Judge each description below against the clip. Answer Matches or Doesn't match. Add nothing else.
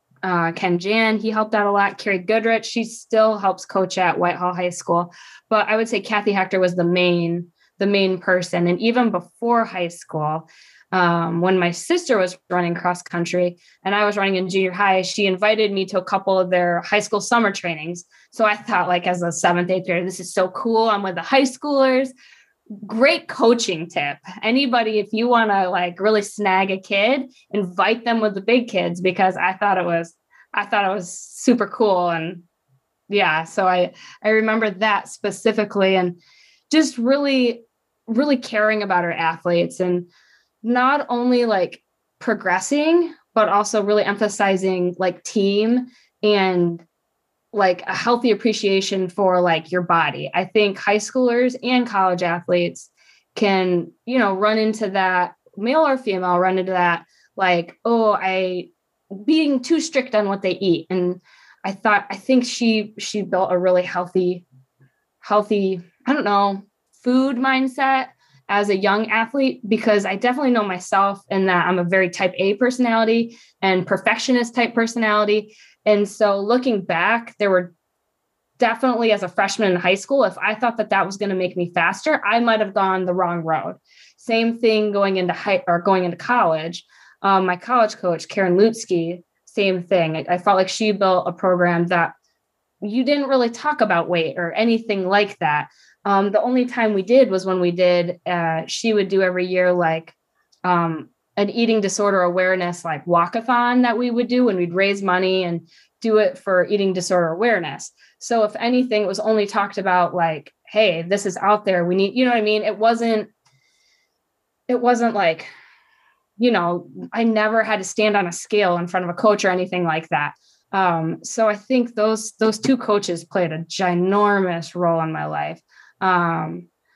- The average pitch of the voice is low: Doesn't match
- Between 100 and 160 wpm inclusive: Doesn't match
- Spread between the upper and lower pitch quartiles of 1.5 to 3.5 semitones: Doesn't match